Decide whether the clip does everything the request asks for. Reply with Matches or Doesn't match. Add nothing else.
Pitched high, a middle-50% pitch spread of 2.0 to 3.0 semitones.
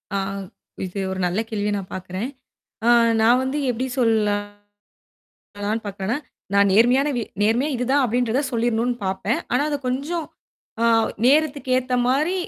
Doesn't match